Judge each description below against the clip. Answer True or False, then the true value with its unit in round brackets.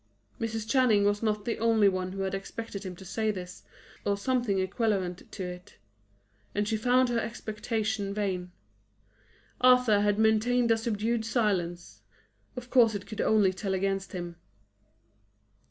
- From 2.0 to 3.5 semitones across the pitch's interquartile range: True (2.8 semitones)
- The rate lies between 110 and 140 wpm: False (150 wpm)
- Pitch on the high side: True (210 Hz)